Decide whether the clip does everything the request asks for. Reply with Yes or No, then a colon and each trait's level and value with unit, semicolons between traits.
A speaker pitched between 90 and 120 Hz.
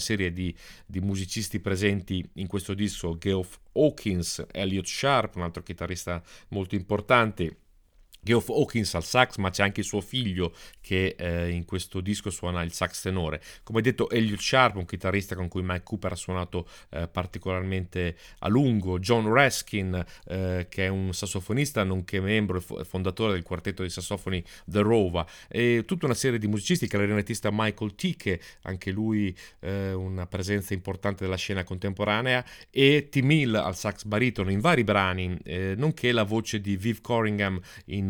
Yes: very low, 95 Hz